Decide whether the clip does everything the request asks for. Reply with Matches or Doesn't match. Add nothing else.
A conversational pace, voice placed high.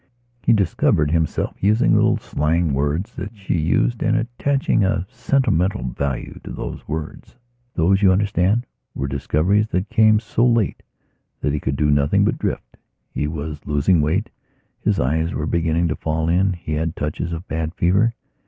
Doesn't match